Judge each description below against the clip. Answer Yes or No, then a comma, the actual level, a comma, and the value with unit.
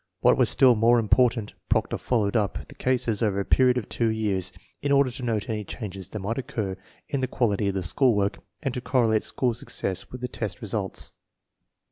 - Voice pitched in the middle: No, low, 115 Hz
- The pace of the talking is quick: Yes, fast, 210 wpm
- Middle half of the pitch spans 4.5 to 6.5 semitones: No, average, 3.6 semitones